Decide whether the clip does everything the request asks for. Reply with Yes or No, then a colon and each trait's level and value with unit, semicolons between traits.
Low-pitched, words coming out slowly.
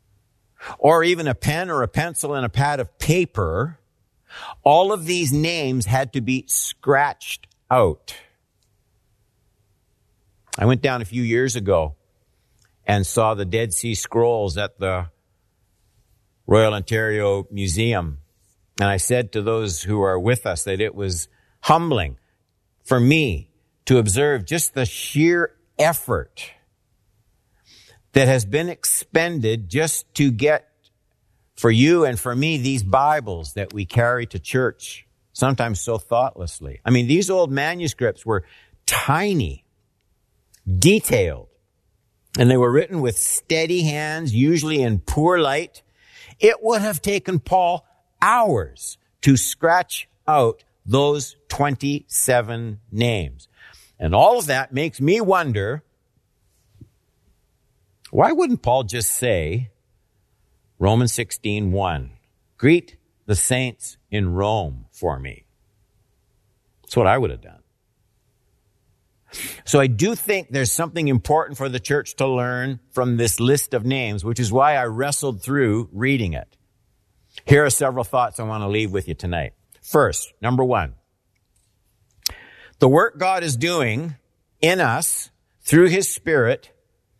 Yes: low, 120 Hz; slow, 130 wpm